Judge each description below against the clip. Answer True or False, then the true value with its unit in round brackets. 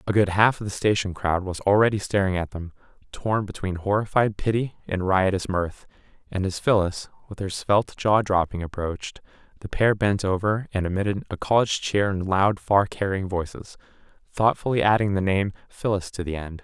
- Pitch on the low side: True (100 Hz)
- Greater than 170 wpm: True (180 wpm)